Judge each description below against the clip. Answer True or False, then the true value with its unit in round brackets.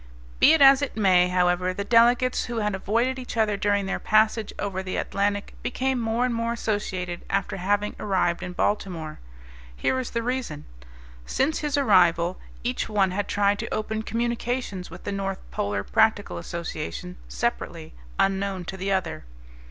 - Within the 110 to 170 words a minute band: True (165 wpm)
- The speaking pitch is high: True (205 Hz)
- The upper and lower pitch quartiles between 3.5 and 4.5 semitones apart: True (4.0 semitones)